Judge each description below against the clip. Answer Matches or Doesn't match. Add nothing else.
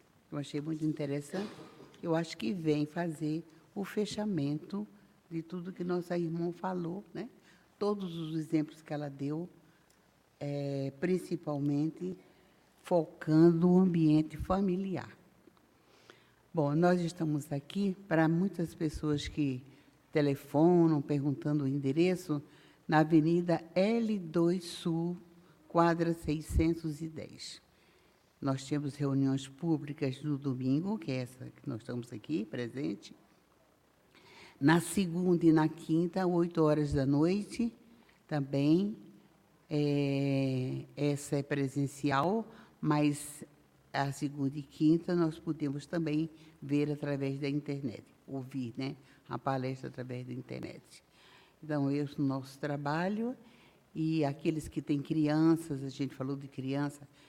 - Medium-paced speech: Doesn't match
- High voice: Doesn't match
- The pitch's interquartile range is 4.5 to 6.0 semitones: Doesn't match